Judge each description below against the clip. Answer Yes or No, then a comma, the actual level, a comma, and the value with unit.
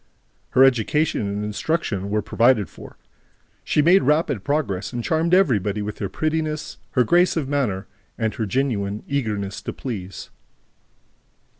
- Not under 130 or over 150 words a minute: Yes, average, 140 wpm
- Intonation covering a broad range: Yes, wide, 6.8 semitones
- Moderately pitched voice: No, low, 120 Hz